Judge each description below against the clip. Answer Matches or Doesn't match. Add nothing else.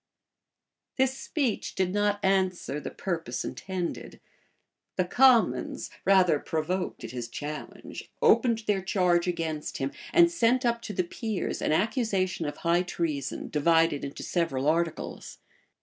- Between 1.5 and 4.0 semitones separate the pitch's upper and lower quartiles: Doesn't match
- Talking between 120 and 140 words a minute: Matches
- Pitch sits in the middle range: Matches